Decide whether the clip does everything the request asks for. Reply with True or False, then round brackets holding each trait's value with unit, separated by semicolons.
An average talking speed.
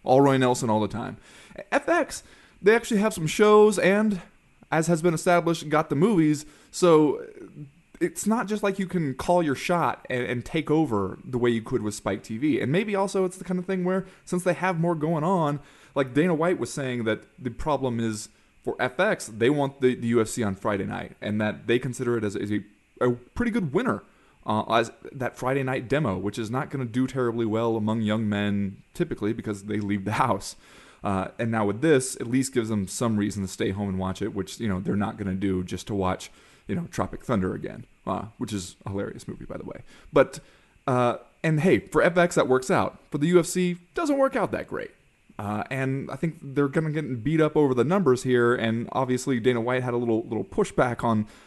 False (225 wpm)